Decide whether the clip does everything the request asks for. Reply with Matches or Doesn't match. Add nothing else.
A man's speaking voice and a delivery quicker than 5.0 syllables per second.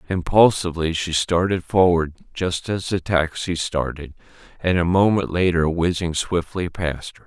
Doesn't match